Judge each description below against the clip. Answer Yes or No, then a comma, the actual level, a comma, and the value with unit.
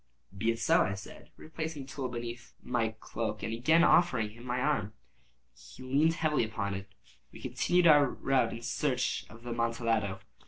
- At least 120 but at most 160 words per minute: No, average, 180 wpm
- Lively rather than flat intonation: No, average, 4.1 semitones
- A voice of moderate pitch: No, low, 120 Hz